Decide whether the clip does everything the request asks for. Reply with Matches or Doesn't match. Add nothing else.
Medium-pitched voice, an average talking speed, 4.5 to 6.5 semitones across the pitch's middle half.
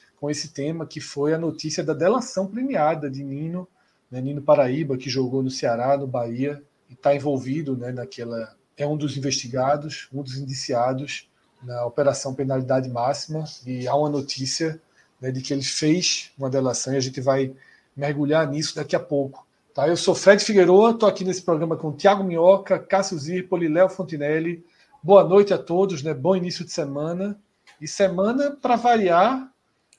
Matches